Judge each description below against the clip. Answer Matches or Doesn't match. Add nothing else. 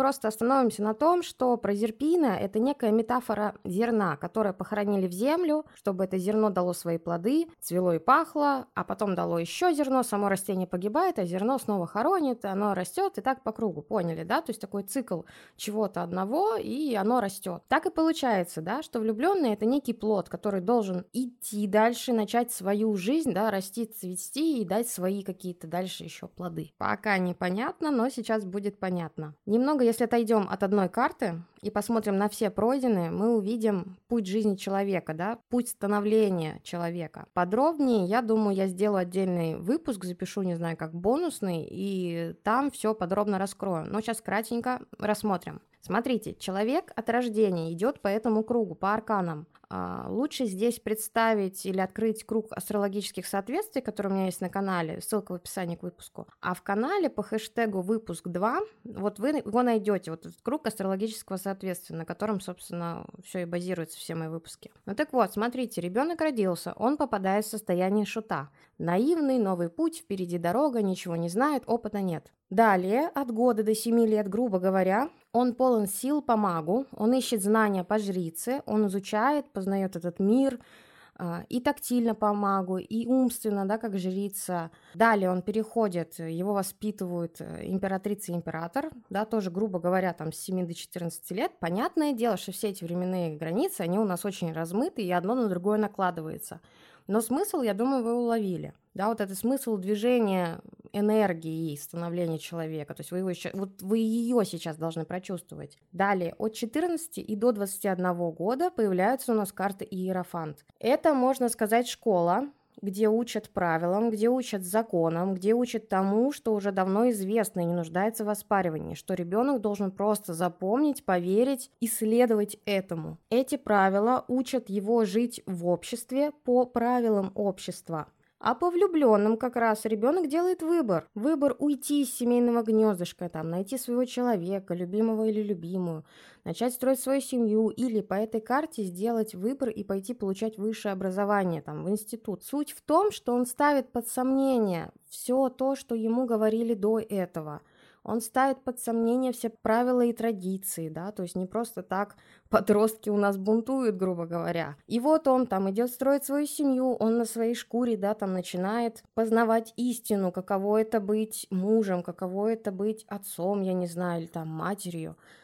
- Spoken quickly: Matches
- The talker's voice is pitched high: Matches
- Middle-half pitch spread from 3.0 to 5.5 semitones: Matches